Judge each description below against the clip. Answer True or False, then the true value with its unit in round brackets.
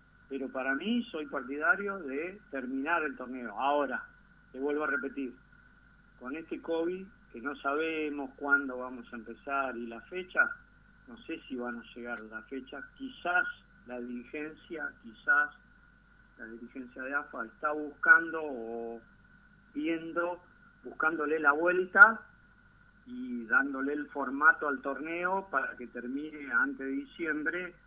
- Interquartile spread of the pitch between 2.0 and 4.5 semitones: False (5.1 semitones)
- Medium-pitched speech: True (145 Hz)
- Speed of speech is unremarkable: True (135 wpm)